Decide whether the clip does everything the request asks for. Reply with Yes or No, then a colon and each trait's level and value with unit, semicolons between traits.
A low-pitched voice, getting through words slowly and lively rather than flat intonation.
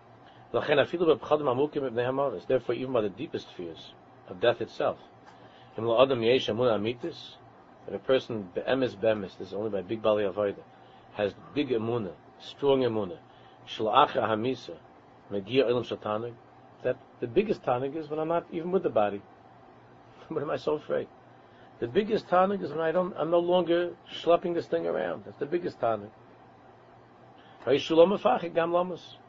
No: low, 130 Hz; average, 170 wpm; wide, 7.1 semitones